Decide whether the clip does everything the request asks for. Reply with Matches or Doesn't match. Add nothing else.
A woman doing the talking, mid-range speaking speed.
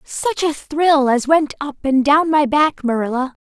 Matches